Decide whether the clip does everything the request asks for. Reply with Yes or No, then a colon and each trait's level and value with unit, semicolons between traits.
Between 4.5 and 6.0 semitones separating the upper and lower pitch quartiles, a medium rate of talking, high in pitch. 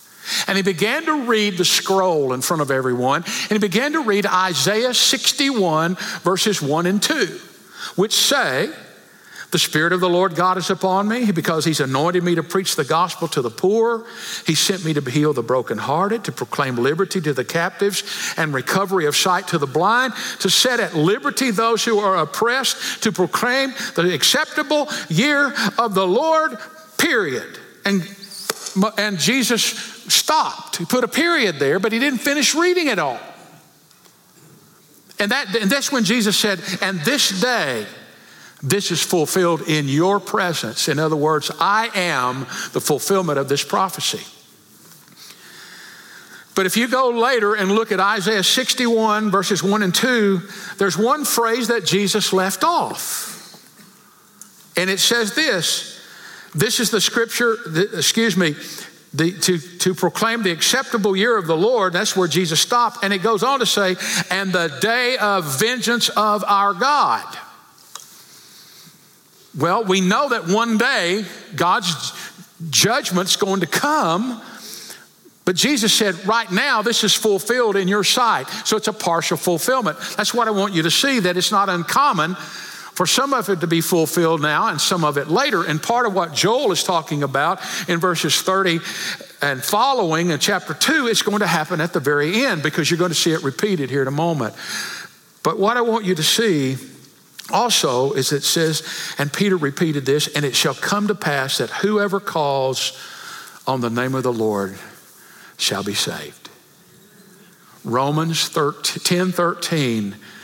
Yes: average, 5.2 semitones; average, 165 wpm; high, 195 Hz